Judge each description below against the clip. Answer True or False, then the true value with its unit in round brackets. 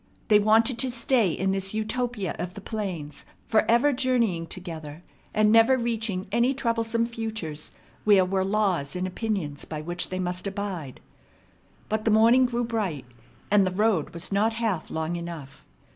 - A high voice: True (205 Hz)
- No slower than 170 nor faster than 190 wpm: False (160 wpm)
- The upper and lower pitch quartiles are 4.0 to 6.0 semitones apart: True (4.4 semitones)